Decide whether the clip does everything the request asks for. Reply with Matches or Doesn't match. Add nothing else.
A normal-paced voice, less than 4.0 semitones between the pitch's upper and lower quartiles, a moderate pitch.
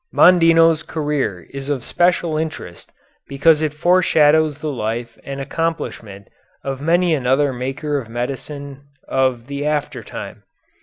Doesn't match